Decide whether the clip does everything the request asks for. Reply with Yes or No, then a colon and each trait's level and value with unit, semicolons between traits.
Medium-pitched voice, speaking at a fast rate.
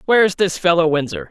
No: medium, 175 Hz; average, 185 wpm